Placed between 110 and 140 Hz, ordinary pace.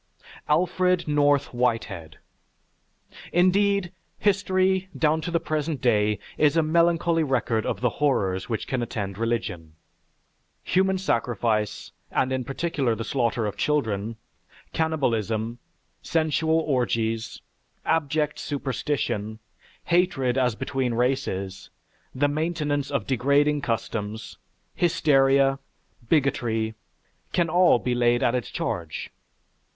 No: low, 135 Hz; slow, 105 wpm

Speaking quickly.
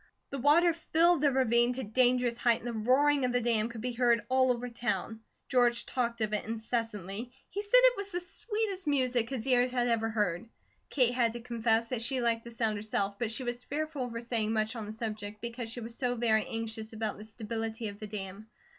Yes: fast, 220 wpm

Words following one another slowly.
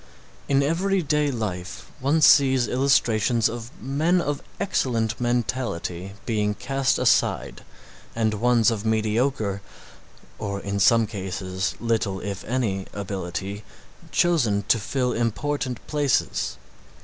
Yes: slow, 110 wpm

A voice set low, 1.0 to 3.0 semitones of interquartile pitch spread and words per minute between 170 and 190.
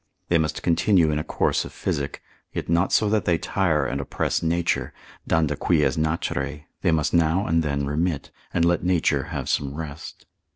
Yes: very low, 80 Hz; average, 2.7 semitones; average, 180 wpm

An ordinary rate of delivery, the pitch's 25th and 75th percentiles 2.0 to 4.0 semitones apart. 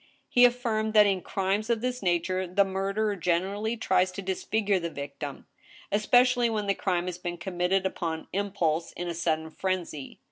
Yes: average, 170 wpm; average, 3.5 semitones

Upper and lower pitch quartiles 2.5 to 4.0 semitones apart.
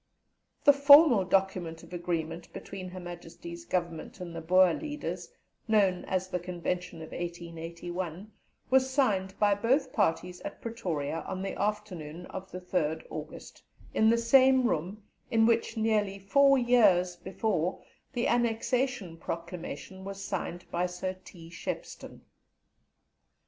No: average, 4.4 semitones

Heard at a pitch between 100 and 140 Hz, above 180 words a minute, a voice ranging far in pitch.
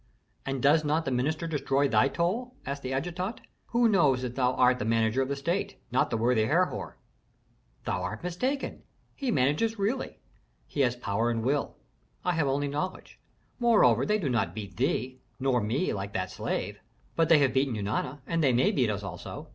Yes: low, 135 Hz; average, 190 wpm; wide, 5.8 semitones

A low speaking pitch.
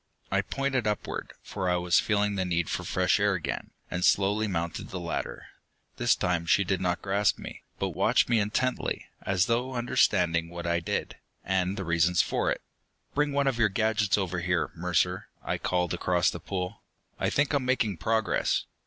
Yes: very low, 95 Hz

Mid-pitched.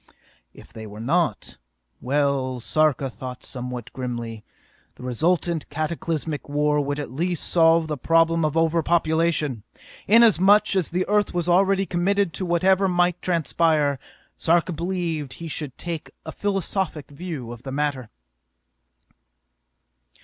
Yes: medium, 160 Hz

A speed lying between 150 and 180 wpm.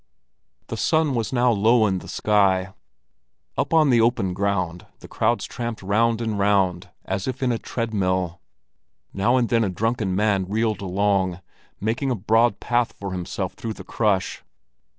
Yes: average, 170 wpm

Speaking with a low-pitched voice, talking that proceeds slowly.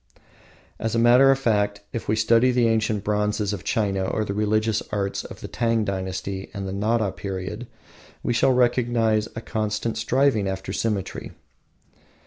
No: low, 110 Hz; average, 160 wpm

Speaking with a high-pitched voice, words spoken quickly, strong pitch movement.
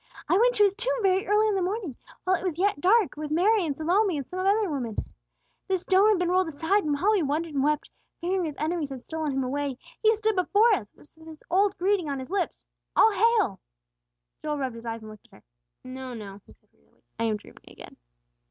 Yes: very high, 345 Hz; fast, 235 wpm; wide, 6.1 semitones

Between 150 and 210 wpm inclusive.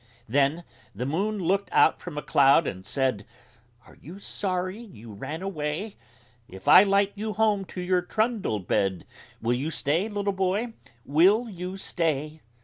Yes: average, 155 wpm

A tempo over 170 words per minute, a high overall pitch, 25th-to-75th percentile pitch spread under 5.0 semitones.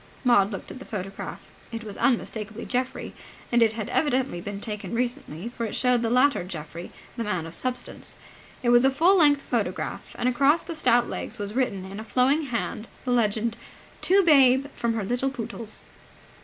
Yes: average, 185 wpm; high, 240 Hz; average, 3.6 semitones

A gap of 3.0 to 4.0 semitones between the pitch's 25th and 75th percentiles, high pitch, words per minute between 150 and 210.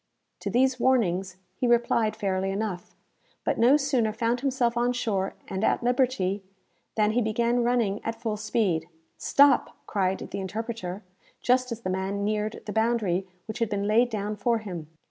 Yes: average, 3.5 semitones; high, 220 Hz; average, 165 wpm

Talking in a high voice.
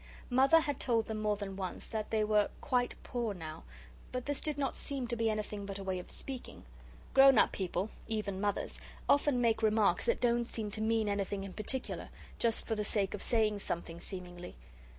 Yes: high, 215 Hz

